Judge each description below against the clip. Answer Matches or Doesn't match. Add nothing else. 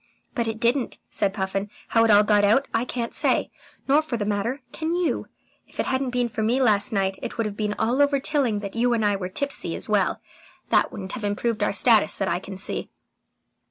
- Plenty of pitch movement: Doesn't match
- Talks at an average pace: Doesn't match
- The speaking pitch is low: Doesn't match